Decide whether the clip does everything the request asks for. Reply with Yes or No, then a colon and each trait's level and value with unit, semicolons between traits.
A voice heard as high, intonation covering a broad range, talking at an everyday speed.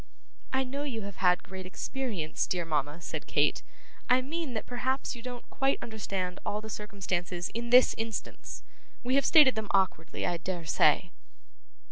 Yes: high, 215 Hz; wide, 6.0 semitones; average, 165 wpm